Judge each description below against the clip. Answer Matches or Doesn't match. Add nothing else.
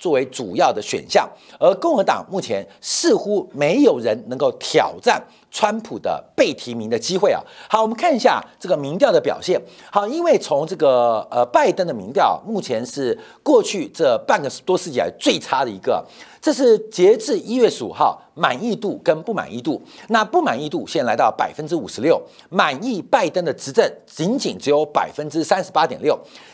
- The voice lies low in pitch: Doesn't match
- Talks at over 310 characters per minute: Doesn't match